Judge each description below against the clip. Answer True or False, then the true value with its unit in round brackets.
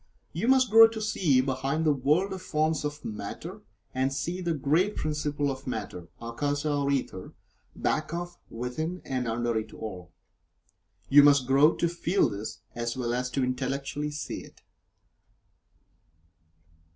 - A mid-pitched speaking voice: True (145 Hz)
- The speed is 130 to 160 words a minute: True (150 wpm)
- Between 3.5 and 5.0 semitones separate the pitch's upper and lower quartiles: True (4.1 semitones)